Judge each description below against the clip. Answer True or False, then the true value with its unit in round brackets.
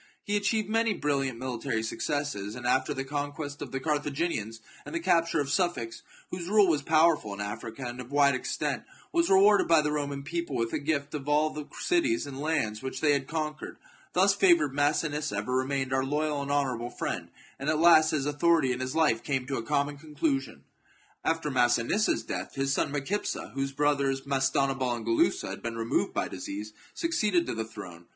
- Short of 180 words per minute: False (195 wpm)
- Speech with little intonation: False (3.7 semitones)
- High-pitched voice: False (145 Hz)